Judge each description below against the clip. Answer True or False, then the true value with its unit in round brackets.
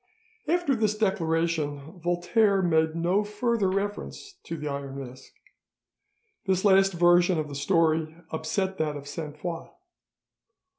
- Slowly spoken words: True (130 wpm)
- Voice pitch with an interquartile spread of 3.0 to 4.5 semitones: True (3.9 semitones)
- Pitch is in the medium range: True (170 Hz)